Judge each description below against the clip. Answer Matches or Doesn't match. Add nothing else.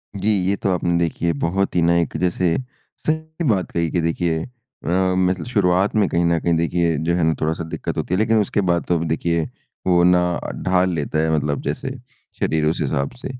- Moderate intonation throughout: Doesn't match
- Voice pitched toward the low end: Matches